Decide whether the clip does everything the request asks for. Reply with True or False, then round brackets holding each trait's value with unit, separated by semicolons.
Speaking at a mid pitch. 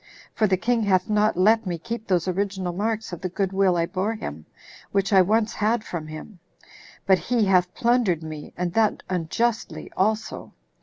False (195 Hz)